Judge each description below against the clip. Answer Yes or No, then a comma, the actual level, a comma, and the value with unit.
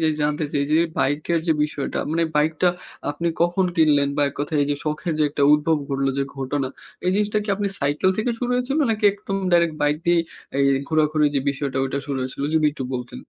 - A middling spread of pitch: Yes, average, 3.3 semitones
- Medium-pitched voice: Yes, medium, 155 Hz